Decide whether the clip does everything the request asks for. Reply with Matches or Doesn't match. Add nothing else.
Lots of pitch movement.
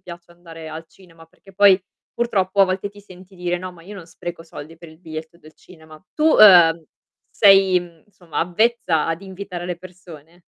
Doesn't match